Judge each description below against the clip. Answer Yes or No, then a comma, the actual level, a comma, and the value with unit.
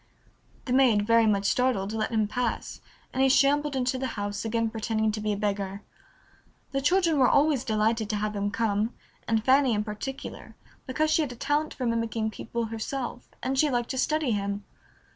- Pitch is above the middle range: Yes, high, 230 Hz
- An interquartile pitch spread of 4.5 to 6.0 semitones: No, average, 3.8 semitones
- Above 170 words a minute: Yes, average, 190 wpm